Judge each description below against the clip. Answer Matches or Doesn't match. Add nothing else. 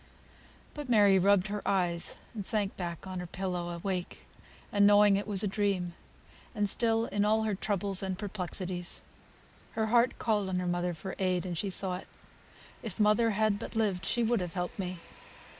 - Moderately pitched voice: Doesn't match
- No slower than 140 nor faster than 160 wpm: Doesn't match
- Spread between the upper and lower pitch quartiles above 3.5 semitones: Doesn't match